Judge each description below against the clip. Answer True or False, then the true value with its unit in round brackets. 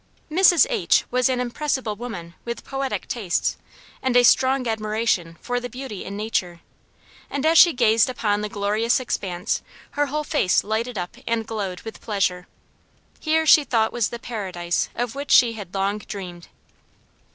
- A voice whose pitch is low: False (225 Hz)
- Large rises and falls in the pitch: False (4.3 semitones)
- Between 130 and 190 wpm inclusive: True (165 wpm)